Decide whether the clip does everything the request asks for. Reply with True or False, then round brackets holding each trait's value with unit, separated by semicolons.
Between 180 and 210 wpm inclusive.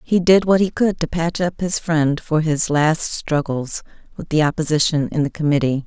True (205 wpm)